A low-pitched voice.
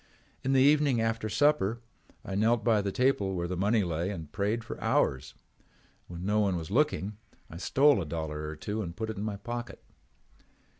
Yes: low, 105 Hz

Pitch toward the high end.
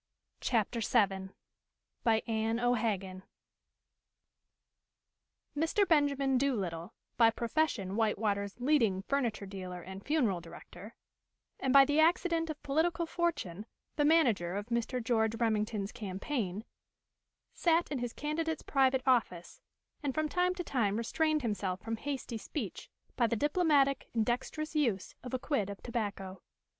Yes: high, 235 Hz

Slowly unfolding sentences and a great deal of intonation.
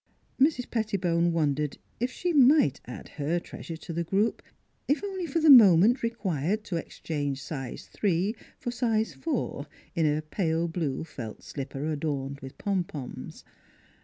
No: average, 145 wpm; wide, 7.5 semitones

